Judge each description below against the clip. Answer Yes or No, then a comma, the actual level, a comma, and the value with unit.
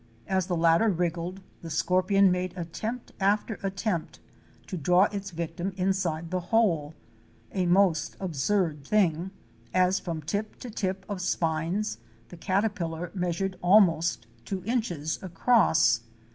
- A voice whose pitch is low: No, medium, 180 Hz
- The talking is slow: Yes, slow, 130 wpm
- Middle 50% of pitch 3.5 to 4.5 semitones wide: No, average, 3.0 semitones